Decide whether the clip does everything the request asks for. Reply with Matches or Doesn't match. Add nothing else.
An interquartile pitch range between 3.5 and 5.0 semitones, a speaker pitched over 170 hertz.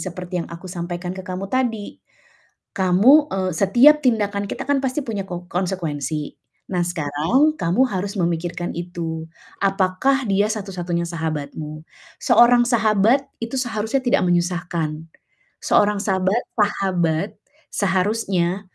Matches